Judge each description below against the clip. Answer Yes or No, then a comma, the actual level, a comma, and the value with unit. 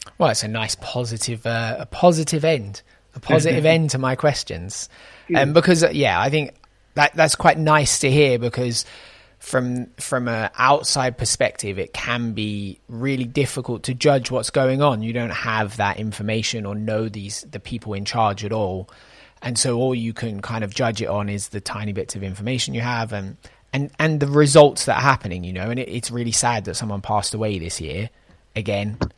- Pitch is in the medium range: No, low, 115 Hz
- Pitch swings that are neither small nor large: Yes, average, 4.1 semitones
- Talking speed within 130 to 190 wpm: No, average, 200 wpm